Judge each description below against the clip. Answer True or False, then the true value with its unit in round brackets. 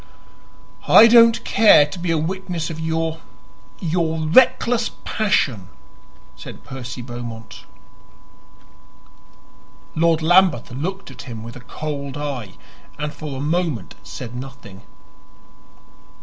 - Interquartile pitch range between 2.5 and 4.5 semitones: False (5.6 semitones)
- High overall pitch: False (155 Hz)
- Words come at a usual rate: False (110 wpm)